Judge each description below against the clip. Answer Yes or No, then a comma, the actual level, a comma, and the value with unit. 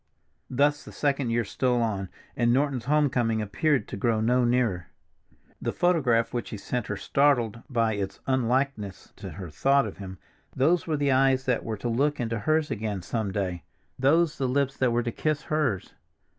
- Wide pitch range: No, average, 4.1 semitones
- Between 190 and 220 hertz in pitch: No, low, 125 Hz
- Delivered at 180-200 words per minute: Yes, average, 185 wpm